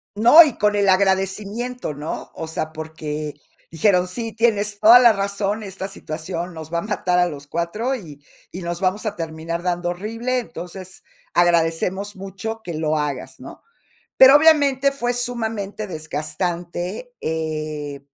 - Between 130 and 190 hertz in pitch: Yes, medium, 185 Hz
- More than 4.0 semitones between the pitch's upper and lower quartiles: Yes, average, 5.1 semitones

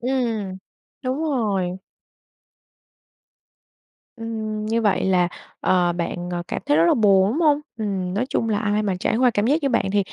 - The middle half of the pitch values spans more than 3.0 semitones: Yes, average, 3.9 semitones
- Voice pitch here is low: No, high, 210 Hz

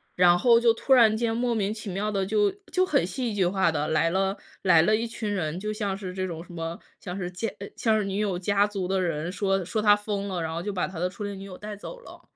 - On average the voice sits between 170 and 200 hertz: Yes, high, 195 Hz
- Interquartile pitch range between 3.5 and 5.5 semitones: No, average, 2.9 semitones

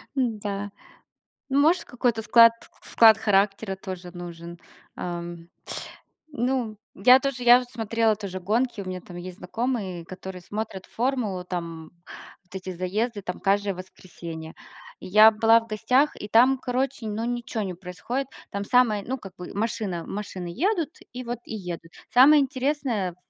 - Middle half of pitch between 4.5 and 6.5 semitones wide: Yes, average, 4.9 semitones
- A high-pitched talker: Yes, high, 210 Hz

